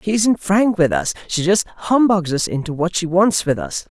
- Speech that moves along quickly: Yes, fast, 225 wpm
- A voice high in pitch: No, medium, 175 Hz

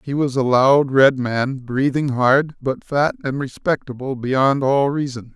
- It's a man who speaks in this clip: Yes, male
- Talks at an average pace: Yes, average, 170 wpm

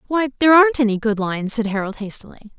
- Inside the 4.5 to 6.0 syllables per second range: No, 6.6 syllables/s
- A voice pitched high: Yes, high, 235 Hz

